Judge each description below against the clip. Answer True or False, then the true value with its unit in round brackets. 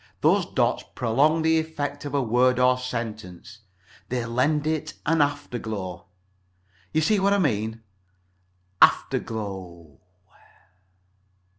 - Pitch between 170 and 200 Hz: False (125 Hz)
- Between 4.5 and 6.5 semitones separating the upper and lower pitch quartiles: True (5.4 semitones)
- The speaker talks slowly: True (110 wpm)